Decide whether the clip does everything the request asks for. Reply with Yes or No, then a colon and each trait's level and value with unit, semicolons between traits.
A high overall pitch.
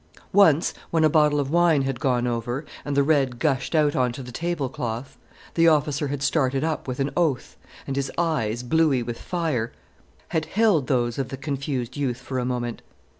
No: low, 135 Hz